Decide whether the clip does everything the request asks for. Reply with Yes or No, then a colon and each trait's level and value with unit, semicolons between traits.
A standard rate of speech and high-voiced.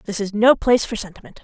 No: fast, 250 wpm; high, 220 Hz